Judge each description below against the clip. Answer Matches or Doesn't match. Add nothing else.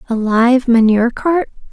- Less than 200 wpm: Matches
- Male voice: Doesn't match